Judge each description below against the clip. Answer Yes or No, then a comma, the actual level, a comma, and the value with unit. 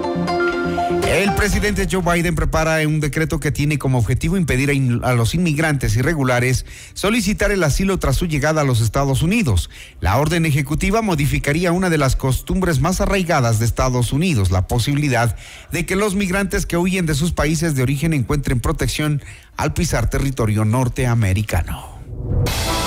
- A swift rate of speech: No, average, 155 wpm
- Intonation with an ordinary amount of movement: No, wide, 6.2 semitones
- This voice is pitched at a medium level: Yes, medium, 145 Hz